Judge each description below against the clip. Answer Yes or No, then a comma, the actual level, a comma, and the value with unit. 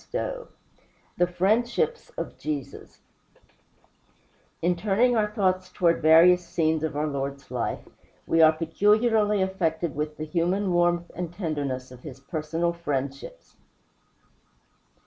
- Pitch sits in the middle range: Yes, medium, 170 Hz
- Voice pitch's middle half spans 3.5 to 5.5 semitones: Yes, average, 3.8 semitones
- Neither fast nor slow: No, slow, 120 wpm